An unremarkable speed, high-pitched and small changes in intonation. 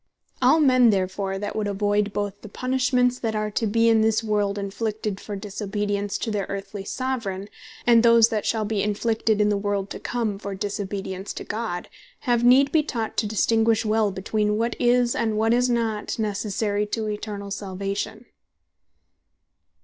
Yes: average, 170 wpm; high, 215 Hz; narrow, 2.2 semitones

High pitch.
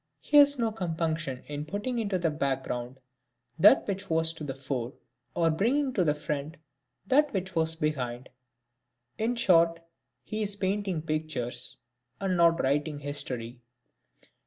No: medium, 160 Hz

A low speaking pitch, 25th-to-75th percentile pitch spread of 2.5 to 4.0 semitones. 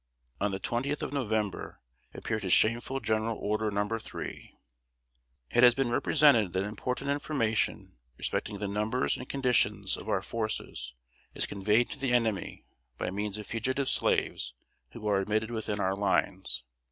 Yes: low, 110 Hz; average, 3.1 semitones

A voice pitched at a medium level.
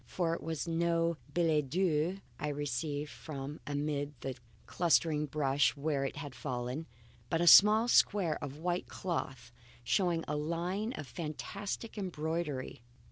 Yes: medium, 155 Hz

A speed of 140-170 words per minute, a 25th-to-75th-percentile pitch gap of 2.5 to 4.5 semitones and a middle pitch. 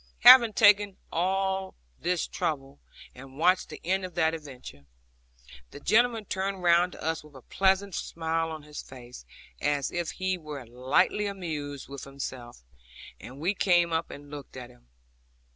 No: average, 160 wpm; average, 5.3 semitones; medium, 165 Hz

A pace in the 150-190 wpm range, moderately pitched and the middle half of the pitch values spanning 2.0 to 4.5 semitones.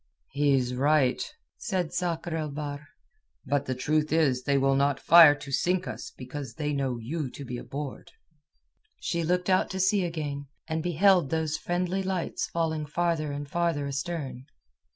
Yes: average, 170 wpm; medium, 150 Hz; average, 3.5 semitones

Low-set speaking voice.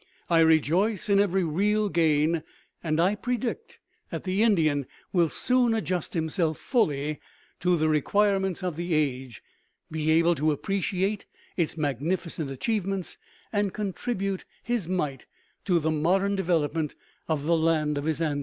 No: medium, 170 Hz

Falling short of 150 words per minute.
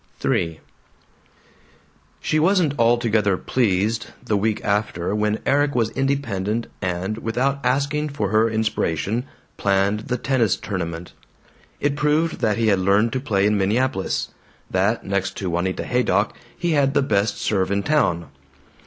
Yes: average, 140 wpm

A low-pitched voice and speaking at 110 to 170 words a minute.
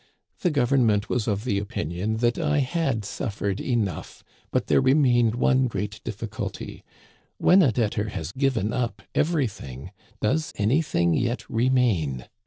Yes: low, 115 Hz; average, 145 wpm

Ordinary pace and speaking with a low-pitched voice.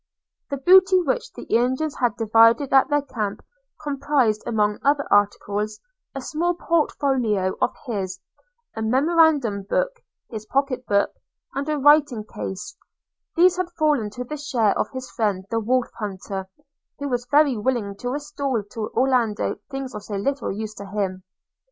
No: average, 155 wpm; very high, 250 Hz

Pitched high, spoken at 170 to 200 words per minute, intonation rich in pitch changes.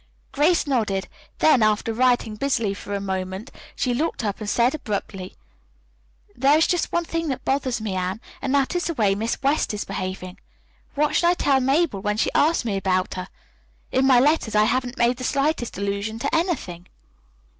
Yes: high, 240 Hz; average, 190 wpm; wide, 5.8 semitones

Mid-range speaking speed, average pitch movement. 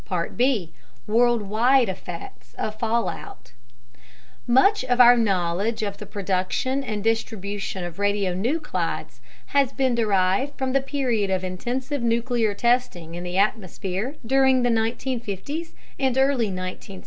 No: slow, 125 wpm; average, 4.9 semitones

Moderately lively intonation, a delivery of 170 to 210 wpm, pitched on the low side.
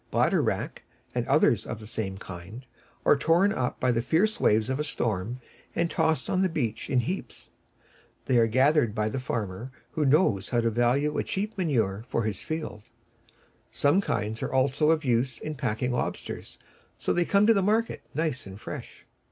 No: wide, 6.1 semitones; average, 190 wpm; low, 130 Hz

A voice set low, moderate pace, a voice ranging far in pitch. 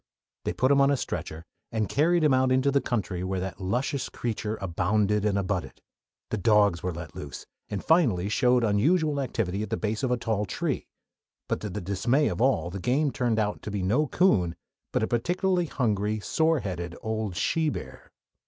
Yes: low, 110 Hz; average, 195 wpm; wide, 5.7 semitones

